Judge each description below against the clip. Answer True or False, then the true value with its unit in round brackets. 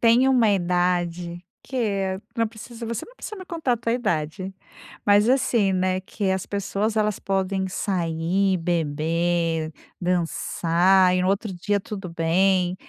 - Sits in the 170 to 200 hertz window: True (190 Hz)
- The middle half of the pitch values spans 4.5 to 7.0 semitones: False (3.4 semitones)